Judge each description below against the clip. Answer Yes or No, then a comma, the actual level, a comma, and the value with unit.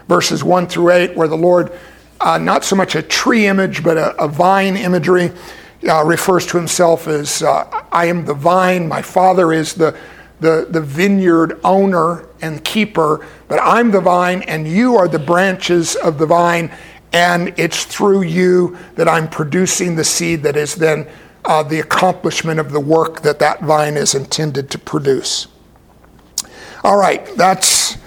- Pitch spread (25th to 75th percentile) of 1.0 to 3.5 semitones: Yes, narrow, 2.4 semitones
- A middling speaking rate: Yes, average, 170 wpm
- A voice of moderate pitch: Yes, medium, 170 Hz